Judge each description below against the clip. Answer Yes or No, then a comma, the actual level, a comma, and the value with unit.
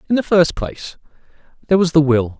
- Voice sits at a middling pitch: Yes, medium, 165 Hz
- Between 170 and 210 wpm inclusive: Yes, average, 200 wpm